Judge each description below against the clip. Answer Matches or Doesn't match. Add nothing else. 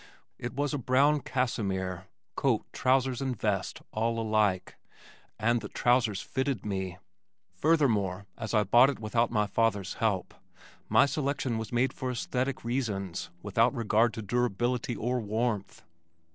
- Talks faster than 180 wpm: Doesn't match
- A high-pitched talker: Doesn't match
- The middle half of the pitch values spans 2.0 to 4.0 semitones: Matches